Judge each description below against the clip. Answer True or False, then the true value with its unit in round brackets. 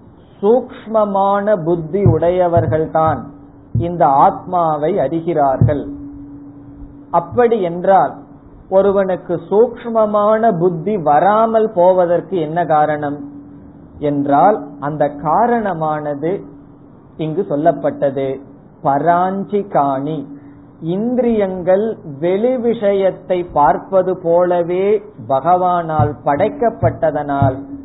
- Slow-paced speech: True (60 wpm)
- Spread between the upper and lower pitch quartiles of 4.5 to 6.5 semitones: True (5.4 semitones)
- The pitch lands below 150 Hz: False (170 Hz)